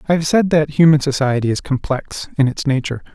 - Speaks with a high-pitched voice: No, medium, 145 Hz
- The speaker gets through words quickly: Yes, fast, 210 wpm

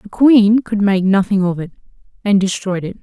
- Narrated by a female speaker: Yes, female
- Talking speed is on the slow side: No, average, 200 wpm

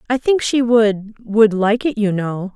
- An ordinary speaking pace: Yes, average, 190 wpm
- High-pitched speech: Yes, high, 220 Hz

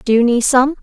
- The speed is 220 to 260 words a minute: No, fast, 290 wpm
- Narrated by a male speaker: No, female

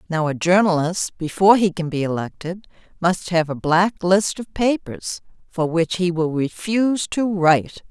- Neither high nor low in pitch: Yes, medium, 180 Hz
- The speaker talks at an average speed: Yes, average, 165 wpm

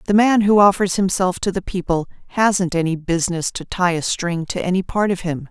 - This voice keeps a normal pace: No, fast, 220 wpm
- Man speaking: No, female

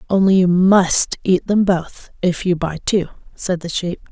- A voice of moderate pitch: Yes, medium, 180 Hz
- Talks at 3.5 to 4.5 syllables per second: Yes, 4.2 syllables/s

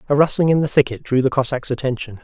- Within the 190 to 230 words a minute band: No, fast, 240 wpm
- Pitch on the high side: No, low, 135 Hz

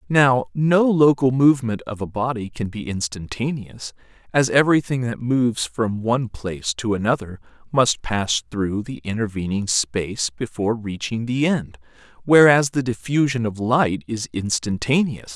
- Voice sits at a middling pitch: No, low, 120 Hz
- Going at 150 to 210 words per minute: No, average, 140 wpm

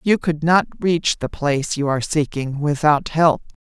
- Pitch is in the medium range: Yes, medium, 150 Hz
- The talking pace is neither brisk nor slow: Yes, average, 180 wpm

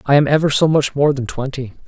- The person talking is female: No, male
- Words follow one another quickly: Yes, fast, 255 wpm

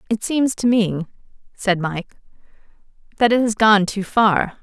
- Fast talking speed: No, average, 155 wpm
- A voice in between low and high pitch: No, high, 210 Hz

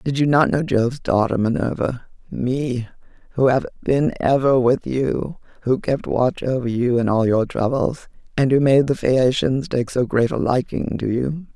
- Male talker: No, female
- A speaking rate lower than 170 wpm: No, average, 175 wpm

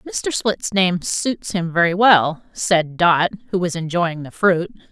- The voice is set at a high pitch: No, medium, 175 Hz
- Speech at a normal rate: Yes, average, 170 wpm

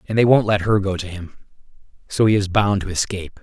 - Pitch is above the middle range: No, low, 100 Hz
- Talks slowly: No, fast, 245 wpm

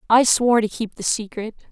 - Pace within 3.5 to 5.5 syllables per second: No, 5.7 syllables/s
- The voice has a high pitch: Yes, high, 225 Hz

